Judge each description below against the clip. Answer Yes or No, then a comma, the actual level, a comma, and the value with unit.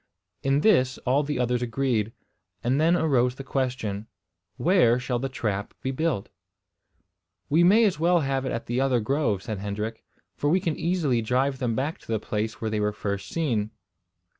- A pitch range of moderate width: Yes, average, 4.7 semitones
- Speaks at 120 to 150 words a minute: No, average, 185 wpm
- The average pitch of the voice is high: No, low, 130 Hz